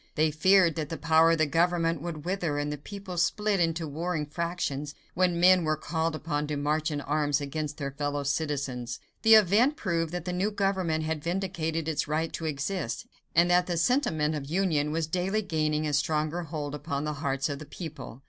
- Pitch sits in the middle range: Yes, medium, 160 Hz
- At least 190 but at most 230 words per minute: Yes, average, 200 wpm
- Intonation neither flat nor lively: Yes, average, 3.0 semitones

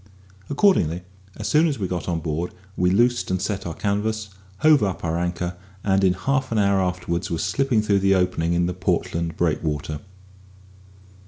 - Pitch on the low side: Yes, very low, 95 Hz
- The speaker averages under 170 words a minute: No, average, 175 wpm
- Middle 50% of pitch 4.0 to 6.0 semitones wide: No, average, 3.6 semitones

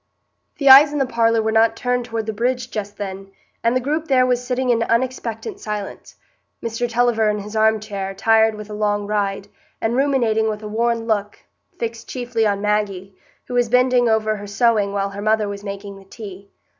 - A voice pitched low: No, high, 220 Hz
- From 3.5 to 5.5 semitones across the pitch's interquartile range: No, average, 2.8 semitones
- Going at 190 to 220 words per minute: Yes, average, 195 wpm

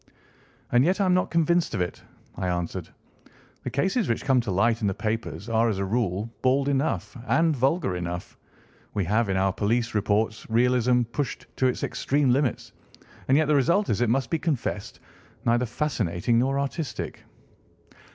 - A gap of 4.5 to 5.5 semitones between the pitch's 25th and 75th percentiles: Yes, average, 5.0 semitones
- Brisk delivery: No, average, 175 wpm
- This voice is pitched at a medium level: No, low, 120 Hz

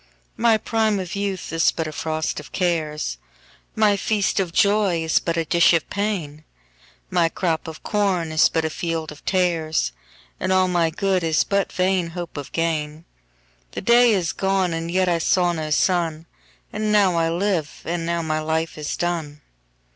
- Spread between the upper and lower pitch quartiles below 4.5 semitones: Yes, average, 3.2 semitones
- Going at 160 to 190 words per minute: Yes, average, 165 wpm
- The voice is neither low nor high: Yes, medium, 170 Hz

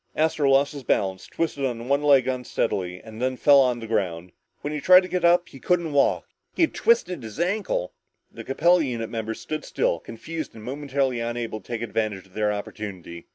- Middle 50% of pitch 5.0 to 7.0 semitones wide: Yes, wide, 5.6 semitones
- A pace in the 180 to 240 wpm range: Yes, average, 200 wpm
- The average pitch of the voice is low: Yes, low, 130 Hz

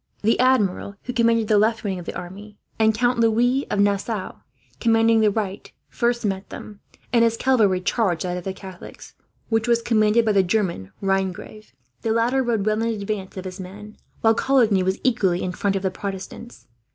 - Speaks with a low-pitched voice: No, high, 215 Hz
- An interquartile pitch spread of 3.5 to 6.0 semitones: No, average, 3.1 semitones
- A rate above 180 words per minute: Yes, average, 190 wpm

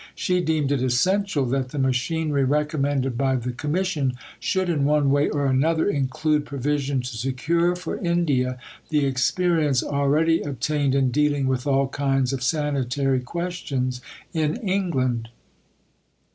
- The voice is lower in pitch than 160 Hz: Yes, medium, 140 Hz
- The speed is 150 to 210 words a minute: No, slow, 135 wpm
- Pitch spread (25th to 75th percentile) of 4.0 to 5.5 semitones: No, average, 3.2 semitones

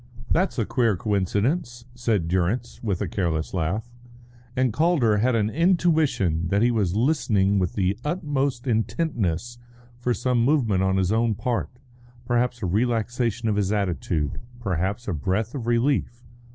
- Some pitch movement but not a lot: Yes, average, 4.3 semitones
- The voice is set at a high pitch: No, low, 115 Hz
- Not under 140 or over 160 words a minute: Yes, average, 150 wpm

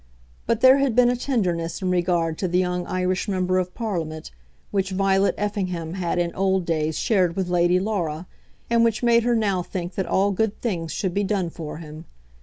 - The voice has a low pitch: No, medium, 185 Hz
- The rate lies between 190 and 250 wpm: Yes, average, 200 wpm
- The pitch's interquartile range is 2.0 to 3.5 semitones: Yes, average, 3.1 semitones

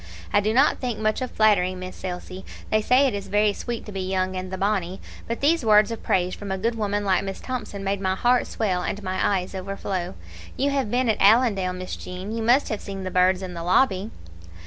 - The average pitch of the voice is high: Yes, high, 200 Hz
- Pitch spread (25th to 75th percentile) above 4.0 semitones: No, average, 3.1 semitones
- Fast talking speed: Yes, fast, 235 wpm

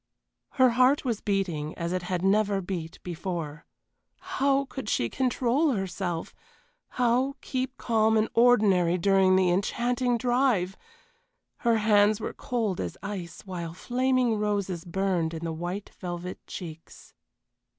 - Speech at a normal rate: No, slow, 130 wpm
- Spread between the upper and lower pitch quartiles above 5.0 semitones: Yes, wide, 5.5 semitones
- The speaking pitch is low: No, high, 200 Hz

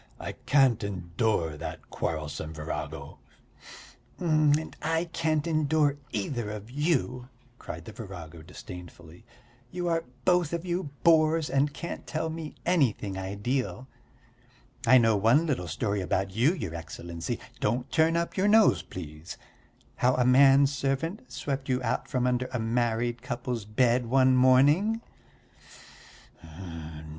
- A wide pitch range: Yes, wide, 7.1 semitones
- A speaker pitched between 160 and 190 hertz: No, low, 125 Hz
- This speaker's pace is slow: Yes, slow, 130 wpm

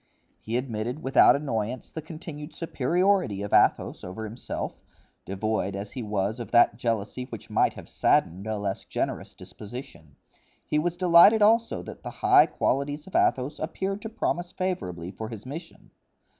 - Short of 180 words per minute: Yes, average, 155 wpm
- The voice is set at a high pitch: No, low, 125 Hz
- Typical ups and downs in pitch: No, wide, 7.9 semitones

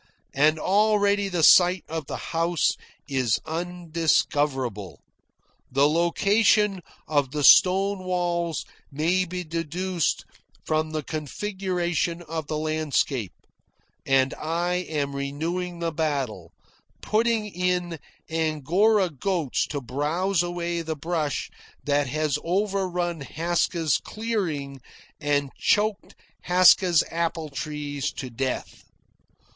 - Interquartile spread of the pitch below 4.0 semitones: Yes, average, 3.6 semitones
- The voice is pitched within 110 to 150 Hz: No, medium, 165 Hz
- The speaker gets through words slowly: Yes, slow, 105 wpm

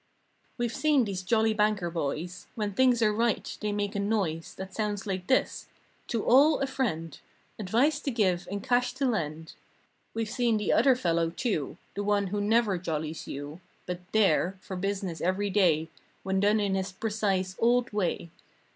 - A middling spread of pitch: Yes, average, 3.9 semitones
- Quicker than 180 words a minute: No, average, 175 wpm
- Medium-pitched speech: No, high, 205 Hz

